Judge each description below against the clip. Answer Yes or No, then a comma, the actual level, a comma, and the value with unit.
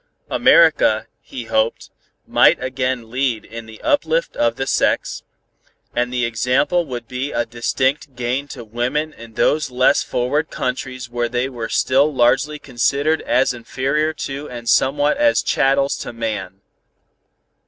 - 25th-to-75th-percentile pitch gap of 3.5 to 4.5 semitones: No, average, 3.1 semitones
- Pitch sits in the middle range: No, low, 130 Hz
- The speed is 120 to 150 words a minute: Yes, average, 145 wpm